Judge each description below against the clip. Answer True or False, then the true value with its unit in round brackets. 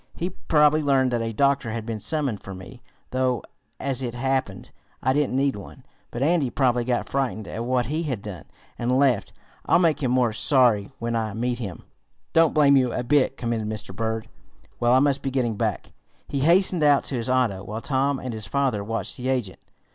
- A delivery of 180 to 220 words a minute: True (205 wpm)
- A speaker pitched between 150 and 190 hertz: False (125 Hz)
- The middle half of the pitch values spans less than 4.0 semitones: True (3.6 semitones)